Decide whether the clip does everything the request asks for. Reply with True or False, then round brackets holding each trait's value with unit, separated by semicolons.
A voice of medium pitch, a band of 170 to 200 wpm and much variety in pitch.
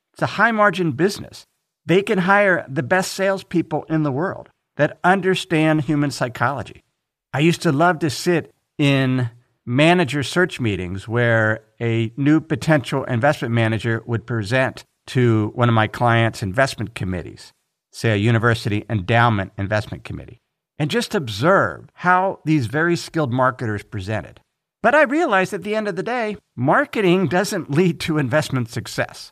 False (145 Hz; 150 wpm; 7.2 semitones)